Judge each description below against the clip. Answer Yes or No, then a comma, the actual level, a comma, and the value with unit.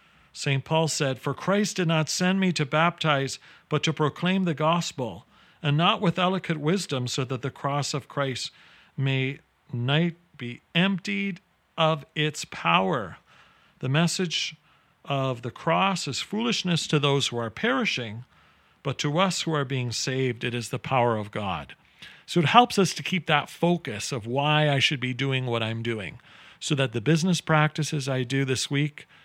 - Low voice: No, medium, 150 Hz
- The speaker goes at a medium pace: Yes, average, 175 wpm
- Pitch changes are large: No, average, 4.3 semitones